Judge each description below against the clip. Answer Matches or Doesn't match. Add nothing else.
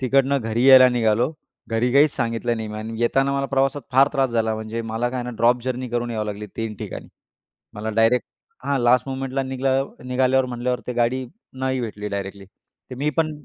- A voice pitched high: Doesn't match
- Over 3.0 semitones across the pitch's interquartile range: Doesn't match